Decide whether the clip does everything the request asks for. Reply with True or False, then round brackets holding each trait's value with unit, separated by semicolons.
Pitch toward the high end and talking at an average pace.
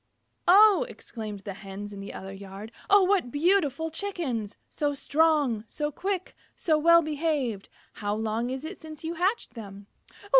True (290 Hz; 155 wpm)